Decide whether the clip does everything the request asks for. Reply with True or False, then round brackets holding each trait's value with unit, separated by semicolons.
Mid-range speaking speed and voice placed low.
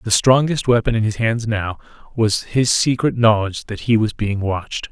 True (195 wpm; 110 Hz)